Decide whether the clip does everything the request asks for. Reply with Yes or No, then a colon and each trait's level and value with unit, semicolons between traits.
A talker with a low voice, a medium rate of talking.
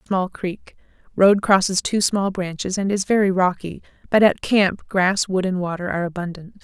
No: high, 190 Hz; average, 170 wpm